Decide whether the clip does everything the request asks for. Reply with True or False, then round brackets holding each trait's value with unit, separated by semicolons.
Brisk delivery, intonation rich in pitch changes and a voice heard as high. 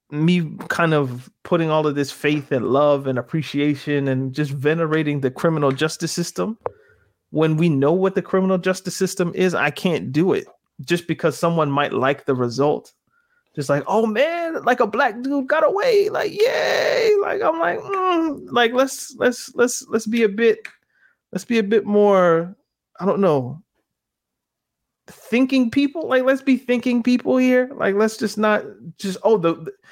False (175 wpm; 8.4 semitones; 195 Hz)